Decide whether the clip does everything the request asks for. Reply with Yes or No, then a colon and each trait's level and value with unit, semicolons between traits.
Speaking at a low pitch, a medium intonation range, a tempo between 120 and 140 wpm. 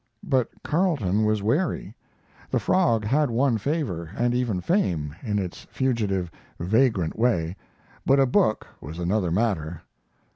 No: low, 110 Hz; wide, 6.5 semitones; slow, 135 wpm